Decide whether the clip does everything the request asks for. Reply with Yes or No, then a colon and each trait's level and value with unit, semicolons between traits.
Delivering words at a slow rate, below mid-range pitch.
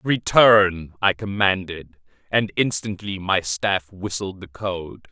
Yes: slow, 115 wpm; very low, 95 Hz